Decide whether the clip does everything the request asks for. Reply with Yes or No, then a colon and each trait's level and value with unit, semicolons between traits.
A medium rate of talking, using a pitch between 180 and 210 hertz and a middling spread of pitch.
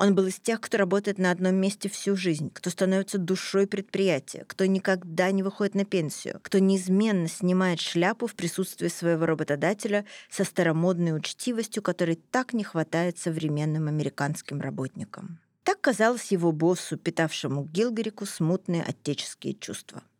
Yes: average, 145 wpm; medium, 185 Hz; average, 3.1 semitones